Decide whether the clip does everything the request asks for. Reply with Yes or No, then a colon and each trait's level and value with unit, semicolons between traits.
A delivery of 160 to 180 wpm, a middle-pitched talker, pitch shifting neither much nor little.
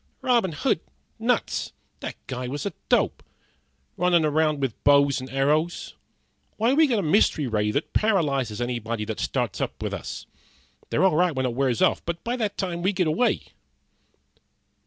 No: average, 170 wpm; medium, 155 Hz; wide, 6.2 semitones